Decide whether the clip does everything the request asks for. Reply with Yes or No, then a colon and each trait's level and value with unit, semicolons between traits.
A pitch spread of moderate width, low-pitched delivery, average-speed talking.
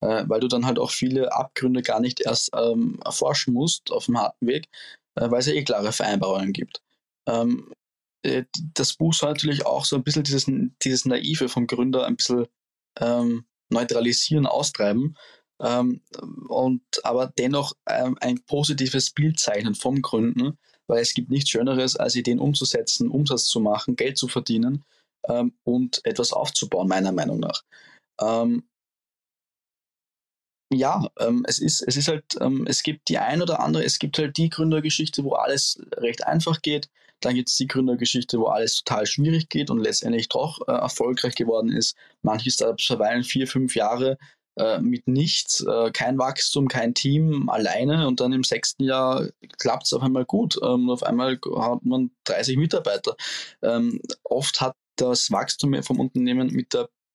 Yes: average, 3.9 semitones; low, 130 Hz; average, 170 wpm